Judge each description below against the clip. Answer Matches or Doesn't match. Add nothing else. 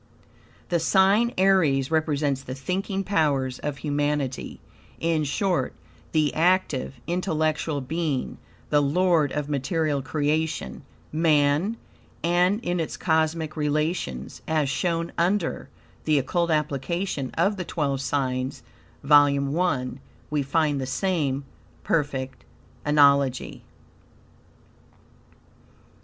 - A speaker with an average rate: Doesn't match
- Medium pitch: Matches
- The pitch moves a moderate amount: Matches